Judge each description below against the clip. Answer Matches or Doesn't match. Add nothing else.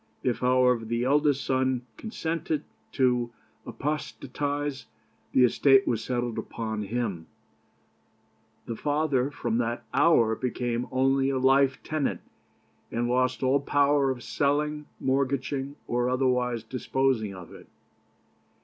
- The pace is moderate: Doesn't match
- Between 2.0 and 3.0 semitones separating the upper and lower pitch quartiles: Matches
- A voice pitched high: Doesn't match